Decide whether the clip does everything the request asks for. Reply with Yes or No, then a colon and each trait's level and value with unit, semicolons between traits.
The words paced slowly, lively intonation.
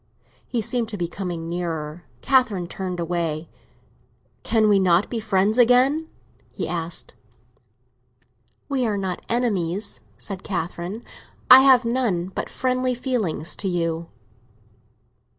Yes: slow, 120 wpm; wide, 5.8 semitones